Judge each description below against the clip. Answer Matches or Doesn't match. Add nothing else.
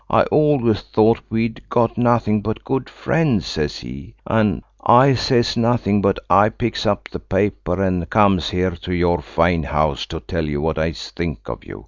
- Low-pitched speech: Matches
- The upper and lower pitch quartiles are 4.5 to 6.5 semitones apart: Matches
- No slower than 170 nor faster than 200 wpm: Matches